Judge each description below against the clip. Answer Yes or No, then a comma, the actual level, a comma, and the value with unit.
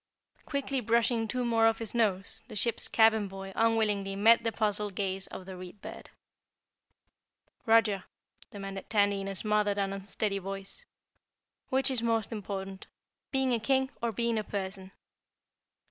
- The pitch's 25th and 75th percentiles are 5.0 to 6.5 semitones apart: No, average, 2.7 semitones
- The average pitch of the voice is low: No, high, 210 Hz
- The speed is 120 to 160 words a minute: Yes, average, 150 wpm